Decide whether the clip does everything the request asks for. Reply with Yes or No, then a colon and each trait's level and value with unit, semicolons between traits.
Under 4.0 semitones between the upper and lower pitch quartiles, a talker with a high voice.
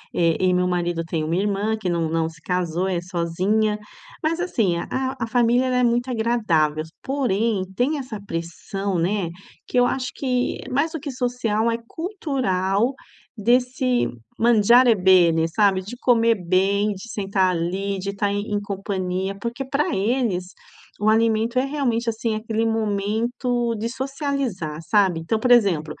No: average, 4.8 semitones; high, 215 Hz